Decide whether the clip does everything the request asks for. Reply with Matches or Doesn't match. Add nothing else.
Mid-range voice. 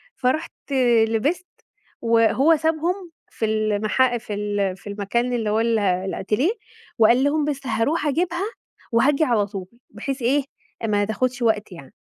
Doesn't match